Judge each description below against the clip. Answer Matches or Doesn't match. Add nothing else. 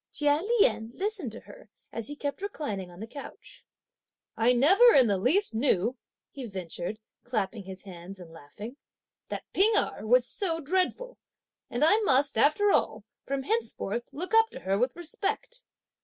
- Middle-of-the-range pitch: Doesn't match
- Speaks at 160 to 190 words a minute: Matches